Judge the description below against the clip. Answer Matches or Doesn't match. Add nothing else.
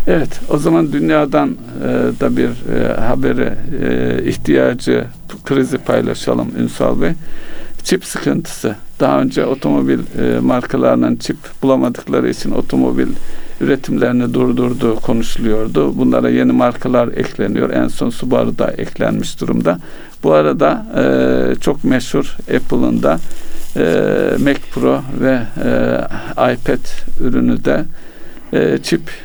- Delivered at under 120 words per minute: Matches